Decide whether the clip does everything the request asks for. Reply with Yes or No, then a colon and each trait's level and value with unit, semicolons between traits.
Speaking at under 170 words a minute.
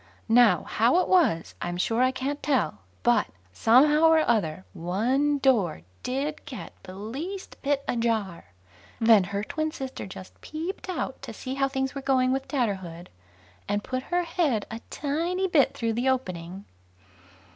Yes: average, 155 wpm